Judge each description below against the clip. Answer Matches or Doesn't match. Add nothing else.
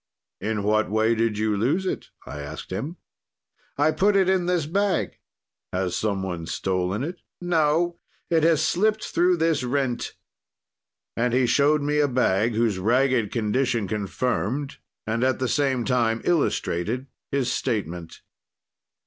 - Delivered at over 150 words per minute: Doesn't match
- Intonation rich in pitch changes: Matches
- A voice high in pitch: Doesn't match